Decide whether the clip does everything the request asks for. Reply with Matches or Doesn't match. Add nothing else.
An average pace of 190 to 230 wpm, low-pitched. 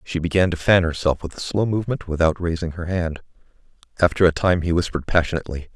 Matches